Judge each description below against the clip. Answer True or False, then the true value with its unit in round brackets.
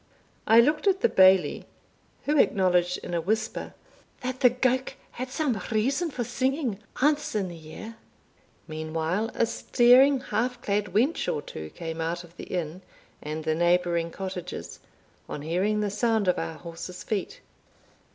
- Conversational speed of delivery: True (155 wpm)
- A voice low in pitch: False (200 Hz)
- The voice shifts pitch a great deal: True (6.5 semitones)